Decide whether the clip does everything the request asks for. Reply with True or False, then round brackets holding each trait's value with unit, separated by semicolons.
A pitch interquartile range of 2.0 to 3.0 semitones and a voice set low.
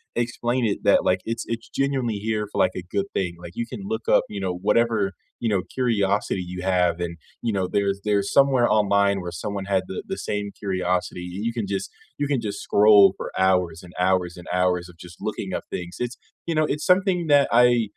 False (4.2 semitones; 100 Hz)